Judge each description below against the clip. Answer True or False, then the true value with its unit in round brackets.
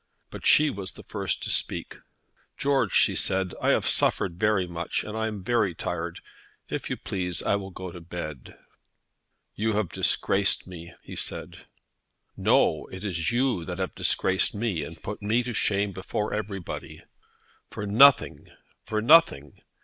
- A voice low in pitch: True (95 Hz)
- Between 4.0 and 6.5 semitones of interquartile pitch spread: False (3.6 semitones)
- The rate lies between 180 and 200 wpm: False (155 wpm)